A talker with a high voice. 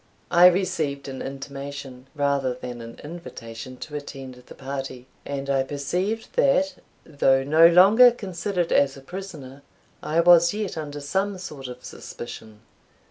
No: medium, 145 Hz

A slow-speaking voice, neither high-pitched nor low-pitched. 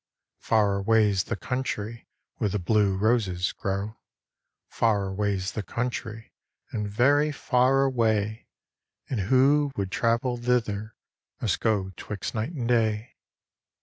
No: slow, 120 wpm; low, 110 Hz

